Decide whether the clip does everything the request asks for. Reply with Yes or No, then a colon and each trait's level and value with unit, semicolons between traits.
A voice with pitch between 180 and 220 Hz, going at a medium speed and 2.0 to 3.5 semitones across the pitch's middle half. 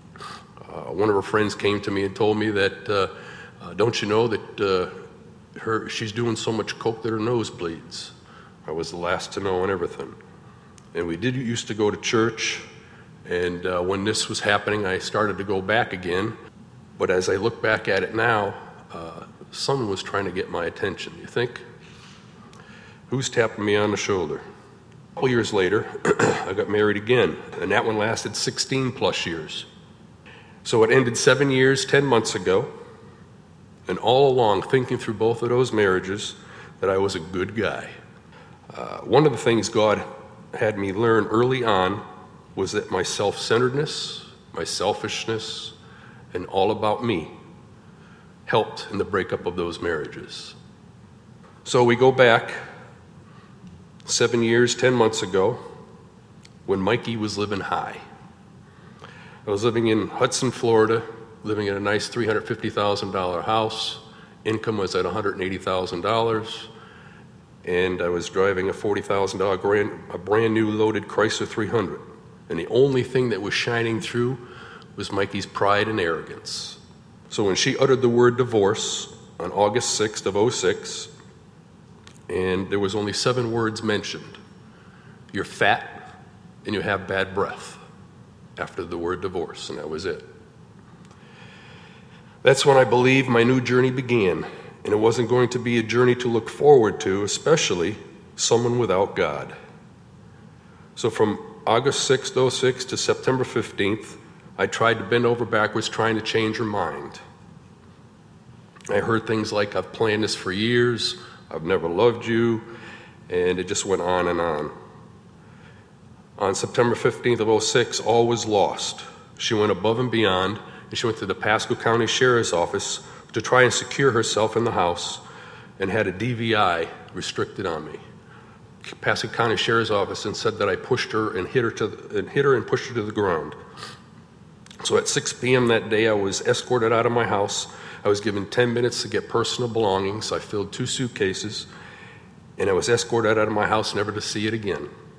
No: low, 115 Hz; average, 170 wpm; average, 3.0 semitones